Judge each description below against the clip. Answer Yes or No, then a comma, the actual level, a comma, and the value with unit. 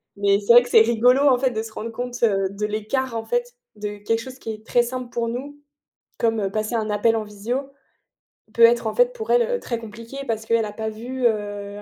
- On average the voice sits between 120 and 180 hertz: No, high, 230 Hz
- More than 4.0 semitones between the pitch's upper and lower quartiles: No, average, 2.7 semitones